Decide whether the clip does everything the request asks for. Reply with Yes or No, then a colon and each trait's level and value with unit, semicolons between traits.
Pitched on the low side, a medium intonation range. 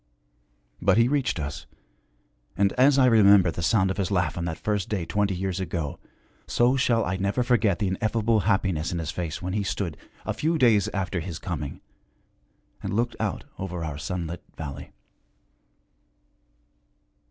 Yes: very low, 95 Hz; average, 4.4 semitones